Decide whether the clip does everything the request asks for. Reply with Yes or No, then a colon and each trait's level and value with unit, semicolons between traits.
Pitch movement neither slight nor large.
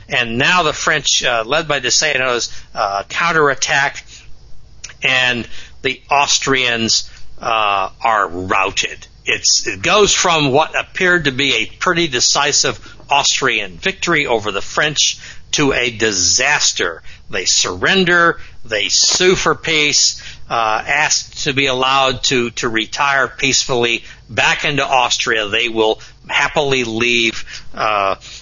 Yes: average, 4.1 semitones